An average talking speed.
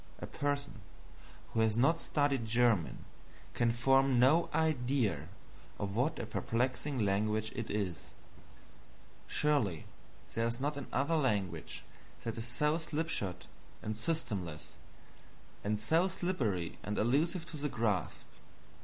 No: slow, 120 wpm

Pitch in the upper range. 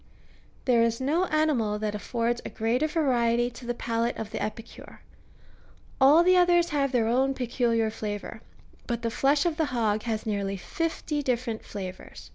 Yes: high, 240 Hz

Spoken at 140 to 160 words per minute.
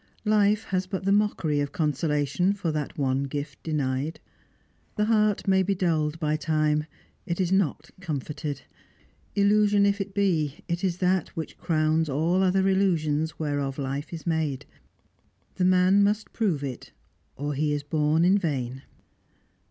Yes: average, 150 wpm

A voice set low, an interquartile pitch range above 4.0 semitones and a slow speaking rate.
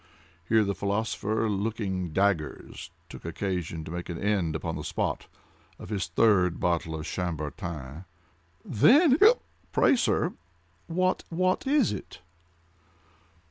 Yes: very low, 95 Hz; average, 5.0 semitones; slow, 110 wpm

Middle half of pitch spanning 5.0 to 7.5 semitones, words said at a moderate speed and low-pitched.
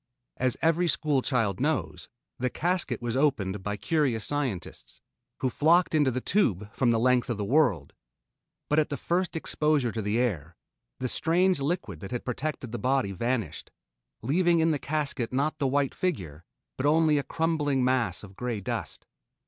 Yes: wide, 5.4 semitones; average, 175 wpm; low, 130 Hz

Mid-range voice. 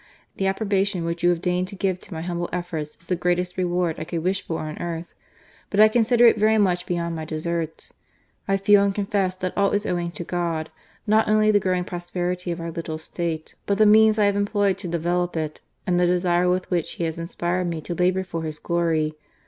Yes: medium, 180 Hz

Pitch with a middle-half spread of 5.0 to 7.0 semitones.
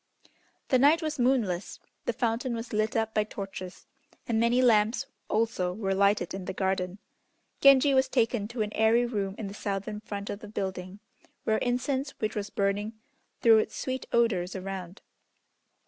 No: average, 3.5 semitones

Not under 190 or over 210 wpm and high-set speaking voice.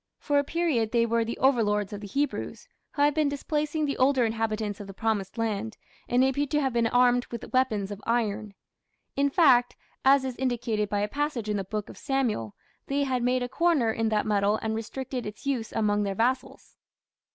Yes: fast, 205 wpm; high, 235 Hz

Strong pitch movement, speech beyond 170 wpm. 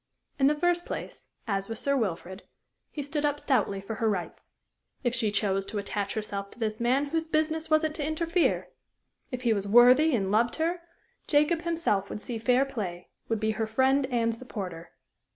Yes: wide, 6.2 semitones; average, 190 wpm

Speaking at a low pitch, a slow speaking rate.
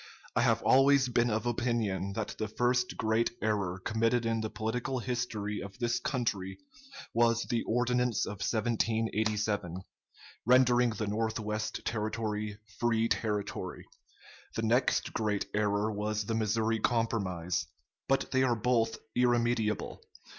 Yes: low, 110 Hz; slow, 130 wpm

